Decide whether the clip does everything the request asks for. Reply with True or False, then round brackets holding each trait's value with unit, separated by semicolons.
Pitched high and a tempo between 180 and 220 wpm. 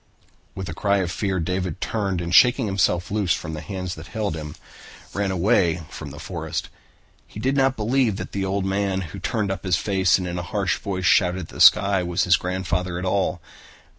False (95 Hz; 205 wpm)